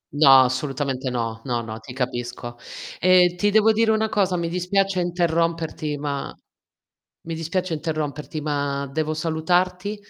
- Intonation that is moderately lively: Yes, average, 4.7 semitones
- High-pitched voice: No, medium, 160 Hz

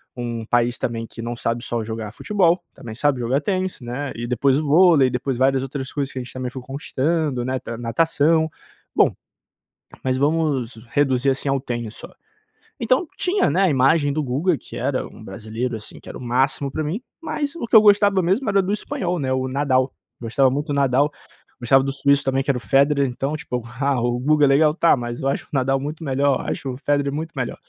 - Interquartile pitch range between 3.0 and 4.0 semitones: Yes, average, 3.6 semitones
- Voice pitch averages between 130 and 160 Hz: Yes, low, 135 Hz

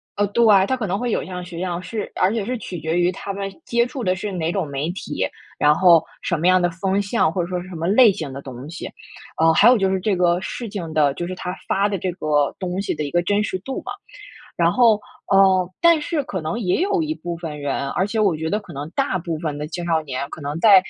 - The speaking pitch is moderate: Yes, medium, 180 Hz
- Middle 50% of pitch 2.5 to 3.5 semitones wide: No, average, 3.9 semitones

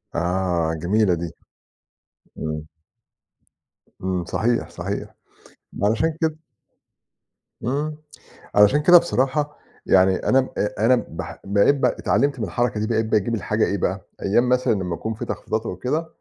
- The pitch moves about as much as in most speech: No, wide, 5.7 semitones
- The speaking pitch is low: Yes, low, 110 Hz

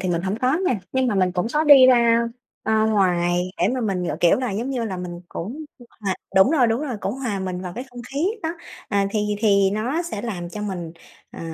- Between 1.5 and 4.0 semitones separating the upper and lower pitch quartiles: No, average, 5.2 semitones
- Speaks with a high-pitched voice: Yes, high, 210 Hz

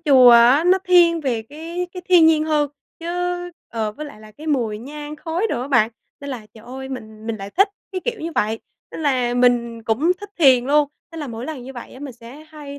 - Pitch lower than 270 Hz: No, very high, 275 Hz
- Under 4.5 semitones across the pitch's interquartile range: No, average, 5.1 semitones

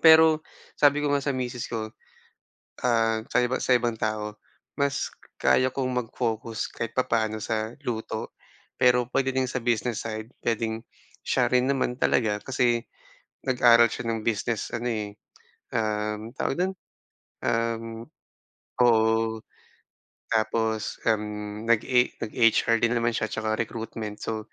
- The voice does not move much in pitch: Yes, narrow, 2.0 semitones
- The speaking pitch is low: Yes, low, 115 Hz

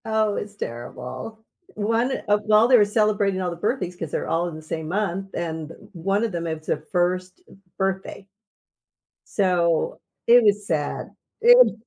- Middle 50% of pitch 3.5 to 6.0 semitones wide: Yes, average, 4.0 semitones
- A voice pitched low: No, high, 195 Hz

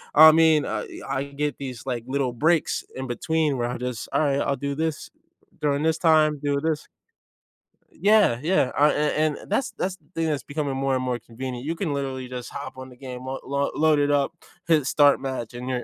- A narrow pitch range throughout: No, average, 3.1 semitones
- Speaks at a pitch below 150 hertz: Yes, medium, 140 Hz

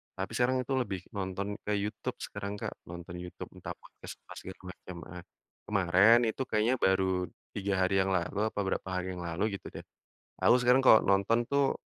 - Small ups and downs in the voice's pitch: No, average, 3.1 semitones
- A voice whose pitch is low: Yes, low, 100 Hz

